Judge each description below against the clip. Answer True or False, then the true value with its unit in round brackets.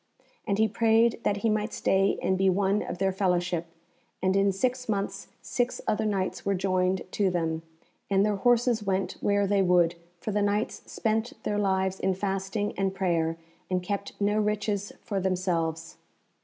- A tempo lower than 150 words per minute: False (170 wpm)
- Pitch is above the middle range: True (195 Hz)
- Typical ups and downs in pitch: False (2.0 semitones)